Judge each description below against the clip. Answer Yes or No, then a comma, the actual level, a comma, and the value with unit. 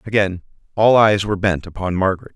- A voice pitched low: Yes, low, 100 Hz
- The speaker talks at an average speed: Yes, average, 180 wpm